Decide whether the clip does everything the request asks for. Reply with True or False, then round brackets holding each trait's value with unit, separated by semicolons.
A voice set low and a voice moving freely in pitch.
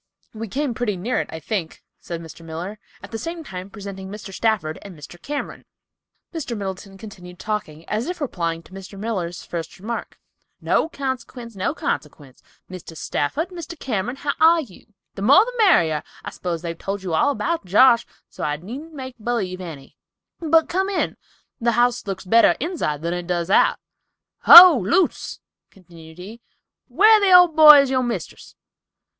False (210 Hz; 7.7 semitones)